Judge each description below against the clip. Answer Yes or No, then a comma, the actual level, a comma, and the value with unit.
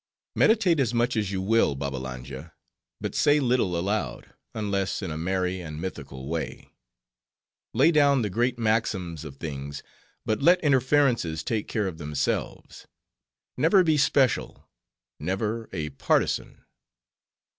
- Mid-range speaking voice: No, low, 100 Hz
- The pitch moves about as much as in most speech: No, wide, 7.9 semitones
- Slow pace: Yes, slow, 130 wpm